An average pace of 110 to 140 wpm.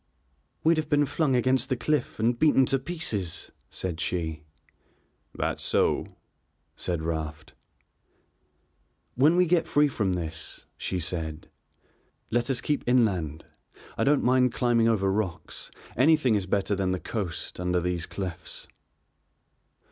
Yes: slow, 135 wpm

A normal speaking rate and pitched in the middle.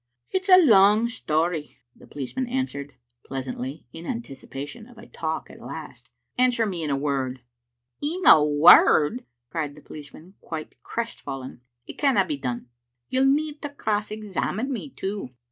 Yes: average, 175 wpm; medium, 170 Hz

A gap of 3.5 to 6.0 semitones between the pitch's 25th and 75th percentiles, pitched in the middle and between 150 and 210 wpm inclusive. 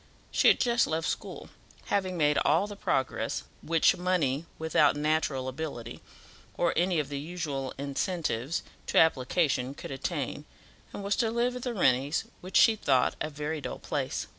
Yes: average, 4.6 semitones; medium, 160 Hz; average, 165 wpm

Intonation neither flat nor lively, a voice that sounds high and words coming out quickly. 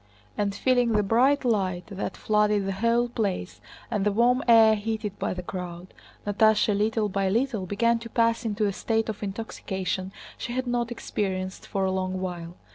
No: average, 3.3 semitones; high, 210 Hz; average, 180 wpm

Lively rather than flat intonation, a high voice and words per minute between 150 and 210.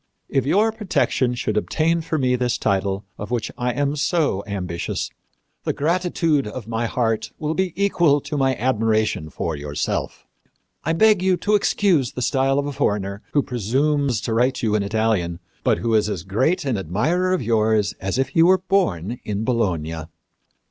No: wide, 6.9 semitones; low, 125 Hz; average, 175 wpm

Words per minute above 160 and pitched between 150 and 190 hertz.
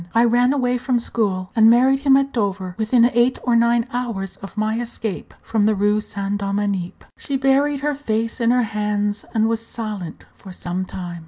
No: average, 190 wpm; high, 225 Hz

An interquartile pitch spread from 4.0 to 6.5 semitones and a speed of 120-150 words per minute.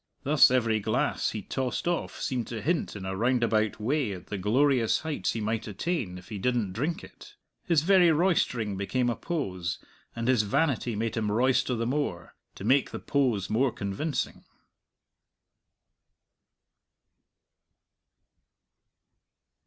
Yes: average, 5.1 semitones; slow, 135 wpm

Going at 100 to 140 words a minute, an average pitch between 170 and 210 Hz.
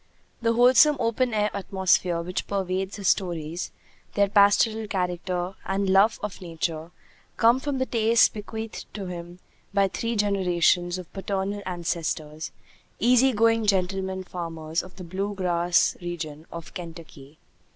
Yes: slow, 135 wpm; high, 190 Hz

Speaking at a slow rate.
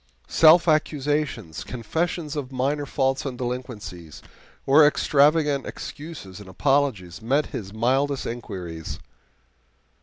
Yes: slow, 100 wpm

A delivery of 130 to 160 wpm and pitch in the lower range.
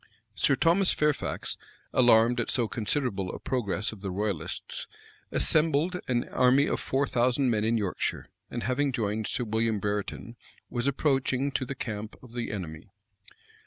Yes: average, 155 wpm; low, 120 Hz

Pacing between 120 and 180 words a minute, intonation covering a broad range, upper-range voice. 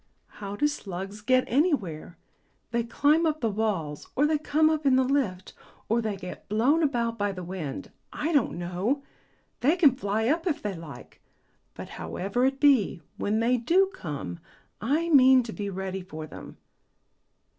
Yes: average, 170 wpm; wide, 6.9 semitones; high, 230 Hz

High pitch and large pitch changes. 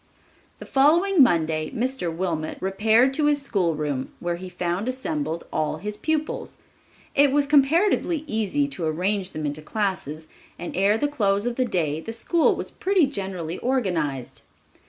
Yes: high, 205 Hz; wide, 8.6 semitones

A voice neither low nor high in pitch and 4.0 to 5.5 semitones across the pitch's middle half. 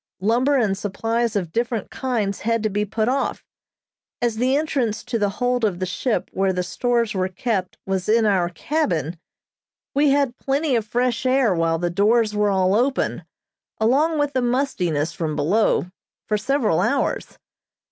No: high, 225 Hz; average, 4.7 semitones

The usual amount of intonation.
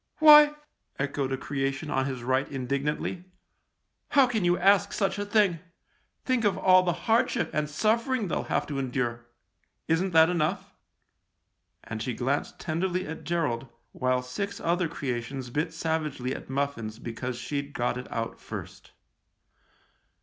No: wide, 6.3 semitones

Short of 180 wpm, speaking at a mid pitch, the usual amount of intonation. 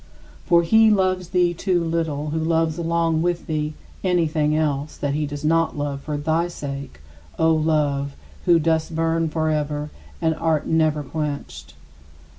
No: average, 150 wpm; medium, 160 Hz; narrow, 1.9 semitones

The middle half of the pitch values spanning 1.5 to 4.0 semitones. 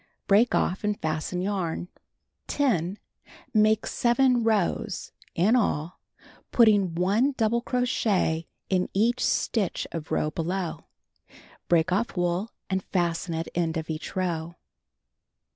No: average, 4.6 semitones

